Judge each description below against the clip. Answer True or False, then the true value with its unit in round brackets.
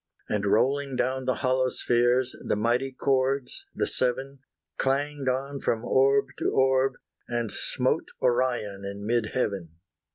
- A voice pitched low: True (130 Hz)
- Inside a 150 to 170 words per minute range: False (135 wpm)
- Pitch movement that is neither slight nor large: False (2.2 semitones)